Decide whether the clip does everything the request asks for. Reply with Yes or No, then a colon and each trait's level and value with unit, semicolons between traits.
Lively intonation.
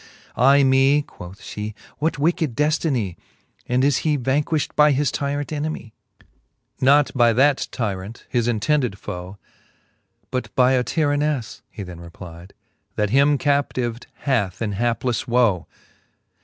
No: average, 4.9 semitones